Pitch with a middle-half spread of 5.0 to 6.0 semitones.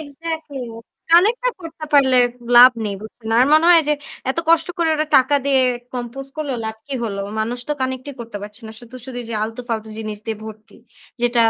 Yes: wide, 5.4 semitones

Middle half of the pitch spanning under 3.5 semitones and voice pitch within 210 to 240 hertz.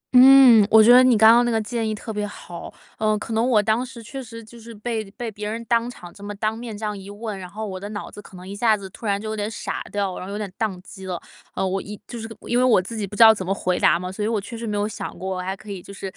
Yes: narrow, 2.5 semitones; high, 215 Hz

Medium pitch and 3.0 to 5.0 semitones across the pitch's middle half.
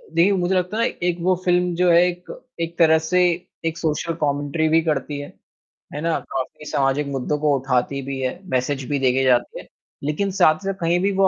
Yes: medium, 160 Hz; average, 4.2 semitones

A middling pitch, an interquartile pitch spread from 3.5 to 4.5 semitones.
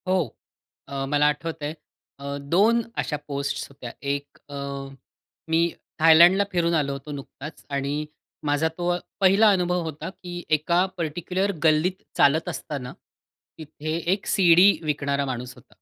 Yes: medium, 160 Hz; average, 3.8 semitones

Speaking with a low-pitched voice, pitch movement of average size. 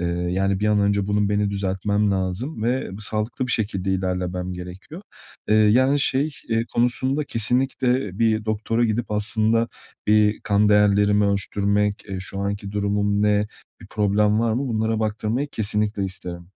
No: low, 105 Hz; narrow, 2.1 semitones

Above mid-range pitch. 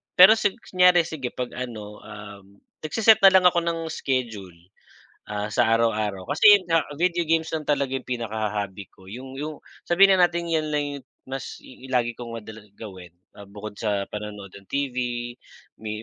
No: low, 125 Hz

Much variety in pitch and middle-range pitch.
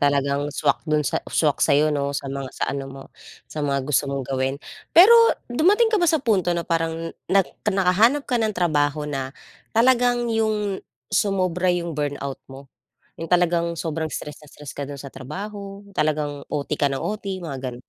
Yes: wide, 6.0 semitones; medium, 160 Hz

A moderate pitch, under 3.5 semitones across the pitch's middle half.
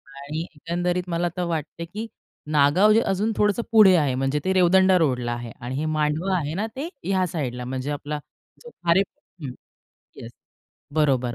No: medium, 165 Hz; average, 5.0 semitones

